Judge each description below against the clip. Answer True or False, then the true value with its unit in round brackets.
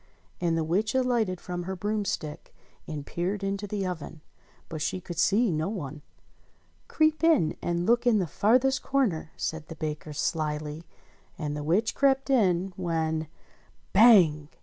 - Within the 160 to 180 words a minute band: False (150 wpm)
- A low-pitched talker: False (180 Hz)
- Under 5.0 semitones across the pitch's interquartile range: False (5.4 semitones)